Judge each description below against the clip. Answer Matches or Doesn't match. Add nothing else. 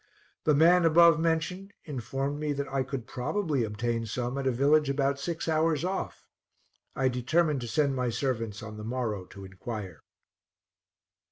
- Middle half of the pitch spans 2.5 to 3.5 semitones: Doesn't match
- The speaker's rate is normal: Matches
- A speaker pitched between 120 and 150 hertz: Matches